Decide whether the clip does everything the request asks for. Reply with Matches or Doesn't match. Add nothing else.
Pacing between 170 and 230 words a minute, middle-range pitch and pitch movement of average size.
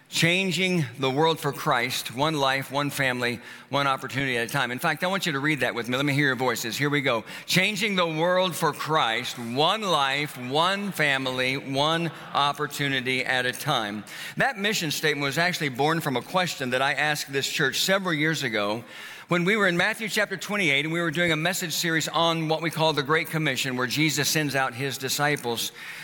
Matches